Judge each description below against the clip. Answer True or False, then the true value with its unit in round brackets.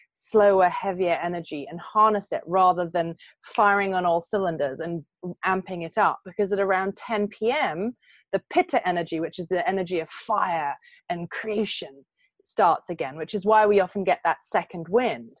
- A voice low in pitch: False (190 Hz)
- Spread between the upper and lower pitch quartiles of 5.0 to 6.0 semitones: False (3.8 semitones)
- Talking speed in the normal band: True (170 wpm)